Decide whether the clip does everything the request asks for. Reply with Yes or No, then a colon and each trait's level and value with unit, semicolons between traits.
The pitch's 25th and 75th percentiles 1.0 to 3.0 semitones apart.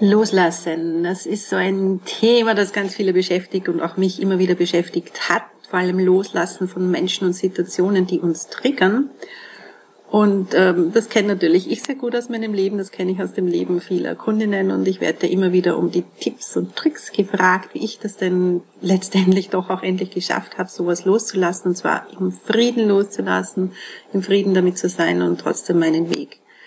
Yes: narrow, 2.4 semitones